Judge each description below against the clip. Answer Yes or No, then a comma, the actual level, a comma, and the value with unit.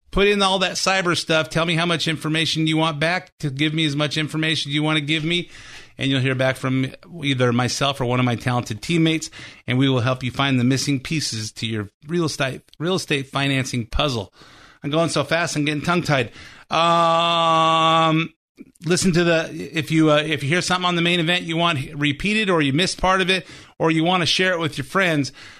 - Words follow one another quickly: Yes, fast, 225 wpm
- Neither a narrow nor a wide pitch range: Yes, average, 3.6 semitones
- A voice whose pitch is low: No, medium, 160 Hz